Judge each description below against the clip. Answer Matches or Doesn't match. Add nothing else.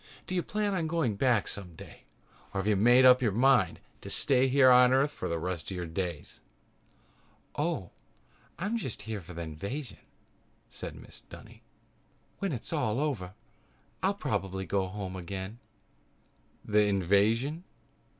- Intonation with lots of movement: Matches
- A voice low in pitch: Matches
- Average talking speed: Matches